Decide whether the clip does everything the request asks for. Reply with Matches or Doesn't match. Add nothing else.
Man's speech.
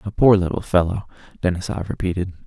Matches